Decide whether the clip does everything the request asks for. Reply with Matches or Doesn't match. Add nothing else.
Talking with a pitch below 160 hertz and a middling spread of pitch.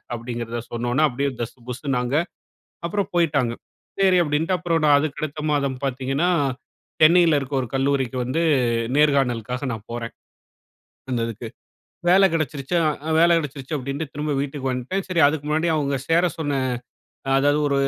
Matches